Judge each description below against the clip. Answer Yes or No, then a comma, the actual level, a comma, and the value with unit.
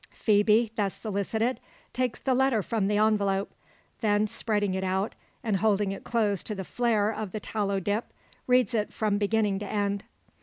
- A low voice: No, high, 210 Hz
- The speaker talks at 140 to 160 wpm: No, average, 175 wpm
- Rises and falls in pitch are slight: Yes, narrow, 1.8 semitones